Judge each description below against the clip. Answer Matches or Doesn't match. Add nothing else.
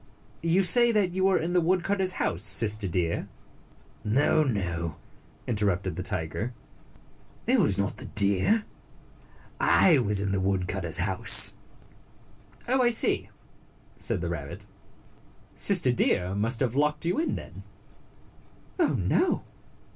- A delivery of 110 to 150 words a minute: Matches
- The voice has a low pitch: Matches